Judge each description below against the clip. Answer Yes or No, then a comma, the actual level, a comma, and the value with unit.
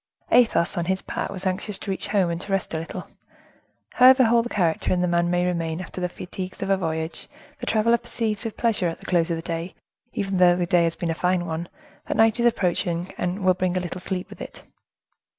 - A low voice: No, medium, 185 Hz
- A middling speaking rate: No, fast, 230 wpm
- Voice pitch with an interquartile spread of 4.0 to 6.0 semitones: No, average, 3.2 semitones